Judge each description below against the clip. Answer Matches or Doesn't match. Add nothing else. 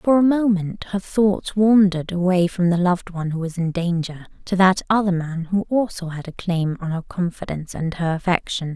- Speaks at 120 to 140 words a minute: Doesn't match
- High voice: Doesn't match